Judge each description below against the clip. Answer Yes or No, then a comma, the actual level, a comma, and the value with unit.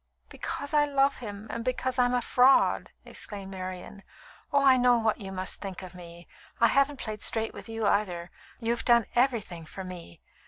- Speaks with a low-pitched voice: No, high, 225 Hz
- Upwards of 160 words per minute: Yes, average, 185 wpm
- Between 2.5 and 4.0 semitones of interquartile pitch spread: No, average, 4.9 semitones